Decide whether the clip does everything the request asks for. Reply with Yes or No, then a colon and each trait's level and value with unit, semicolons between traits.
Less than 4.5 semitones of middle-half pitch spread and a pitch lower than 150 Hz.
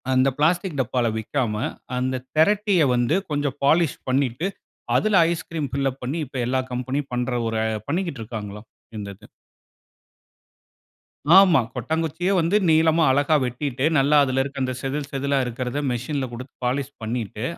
Yes: average, 4.0 semitones; low, 135 Hz